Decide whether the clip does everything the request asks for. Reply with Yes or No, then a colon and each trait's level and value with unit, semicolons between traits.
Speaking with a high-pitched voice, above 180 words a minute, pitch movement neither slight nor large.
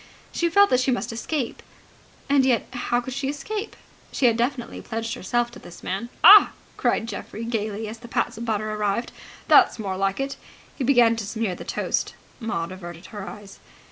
Yes: high, 230 Hz; average, 190 wpm; average, 3.6 semitones